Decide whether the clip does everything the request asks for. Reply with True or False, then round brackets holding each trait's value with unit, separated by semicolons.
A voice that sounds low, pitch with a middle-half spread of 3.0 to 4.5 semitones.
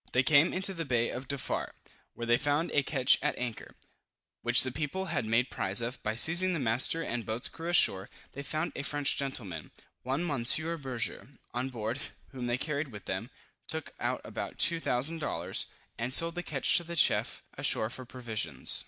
False (130 Hz; 4.9 semitones)